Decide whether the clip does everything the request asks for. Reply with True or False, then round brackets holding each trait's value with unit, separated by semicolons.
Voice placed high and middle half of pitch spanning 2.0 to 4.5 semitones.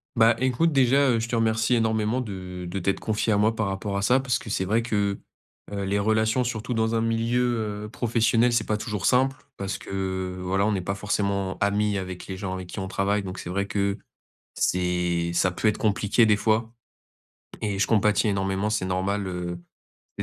False (105 Hz; 2.8 semitones)